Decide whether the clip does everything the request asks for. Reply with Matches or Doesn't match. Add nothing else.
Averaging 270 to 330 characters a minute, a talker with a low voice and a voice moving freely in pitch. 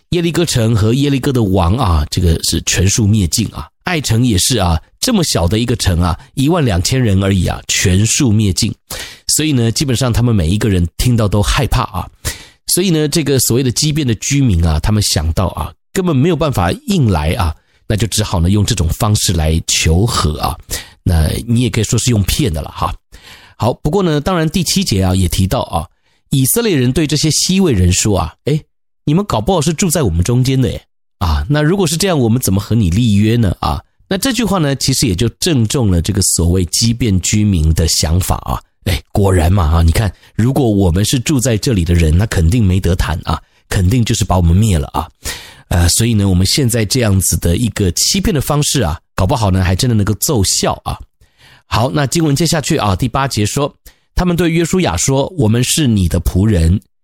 Matches